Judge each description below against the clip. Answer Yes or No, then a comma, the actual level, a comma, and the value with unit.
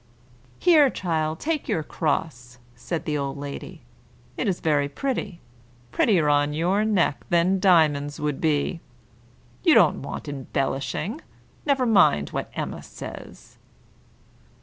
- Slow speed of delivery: Yes, slow, 125 wpm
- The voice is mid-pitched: Yes, medium, 160 Hz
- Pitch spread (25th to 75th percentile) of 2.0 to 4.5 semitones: No, average, 5.2 semitones